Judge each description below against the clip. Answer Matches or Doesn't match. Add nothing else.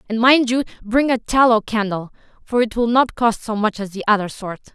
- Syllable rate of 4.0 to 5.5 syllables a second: Matches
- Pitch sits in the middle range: Doesn't match